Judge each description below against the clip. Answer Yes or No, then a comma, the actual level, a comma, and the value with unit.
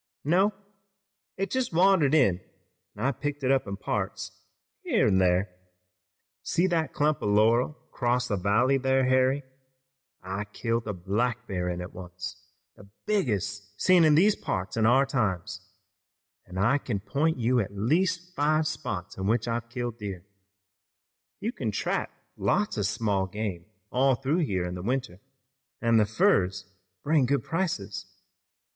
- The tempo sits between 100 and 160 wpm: Yes, average, 155 wpm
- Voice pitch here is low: Yes, low, 115 Hz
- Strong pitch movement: Yes, wide, 6.5 semitones